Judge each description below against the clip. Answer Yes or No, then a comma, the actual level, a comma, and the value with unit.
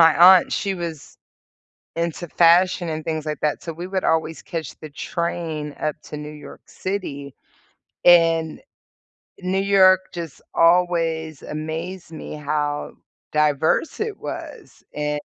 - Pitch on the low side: No, medium, 165 Hz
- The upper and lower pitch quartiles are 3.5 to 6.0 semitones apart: No, narrow, 2.5 semitones